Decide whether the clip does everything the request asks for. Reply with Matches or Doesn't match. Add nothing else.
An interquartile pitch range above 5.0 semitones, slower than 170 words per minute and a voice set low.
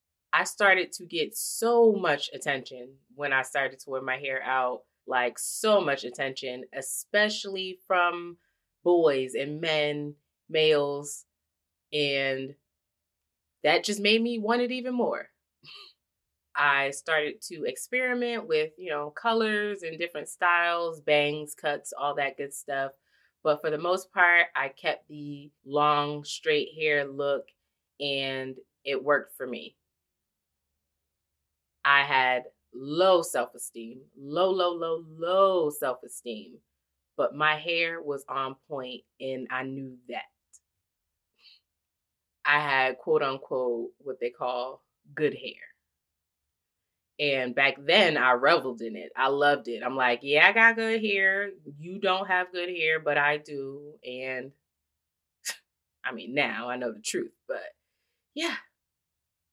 Doesn't match